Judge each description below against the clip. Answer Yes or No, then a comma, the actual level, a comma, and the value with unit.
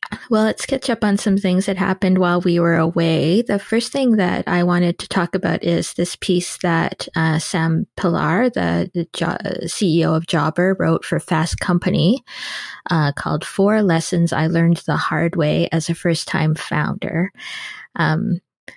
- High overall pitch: No, medium, 175 Hz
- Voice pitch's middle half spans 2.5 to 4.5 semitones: Yes, average, 2.8 semitones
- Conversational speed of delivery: Yes, average, 175 wpm